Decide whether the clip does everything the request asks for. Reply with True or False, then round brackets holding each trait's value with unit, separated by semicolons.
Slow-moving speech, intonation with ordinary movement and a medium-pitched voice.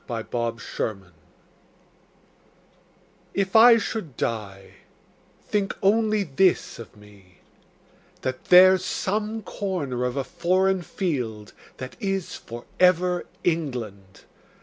False (100 wpm; 8.8 semitones; 165 Hz)